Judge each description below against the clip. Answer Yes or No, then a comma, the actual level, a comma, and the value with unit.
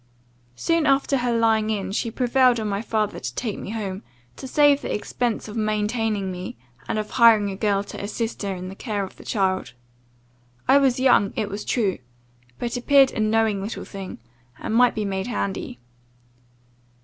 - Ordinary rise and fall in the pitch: Yes, average, 3.5 semitones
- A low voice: No, high, 220 Hz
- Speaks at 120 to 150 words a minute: No, average, 185 wpm